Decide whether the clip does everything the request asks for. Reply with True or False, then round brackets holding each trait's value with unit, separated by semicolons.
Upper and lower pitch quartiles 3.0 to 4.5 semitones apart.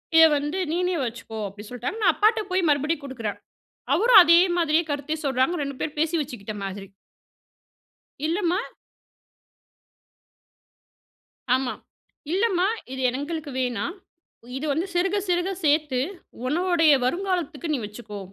False (5.3 semitones)